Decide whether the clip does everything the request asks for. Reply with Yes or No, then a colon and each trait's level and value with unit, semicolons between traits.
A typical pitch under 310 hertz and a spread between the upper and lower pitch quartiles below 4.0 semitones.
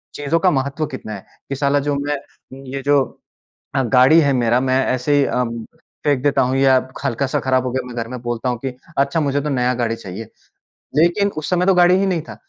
Yes: low, 135 Hz; narrow, 2.6 semitones